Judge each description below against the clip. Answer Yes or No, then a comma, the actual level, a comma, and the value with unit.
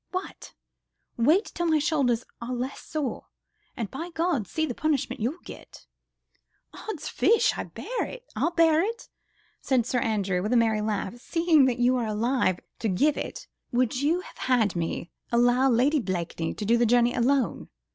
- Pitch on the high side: Yes, very high, 250 Hz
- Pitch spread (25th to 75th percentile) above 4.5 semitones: Yes, wide, 5.5 semitones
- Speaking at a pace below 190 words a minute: Yes, average, 165 wpm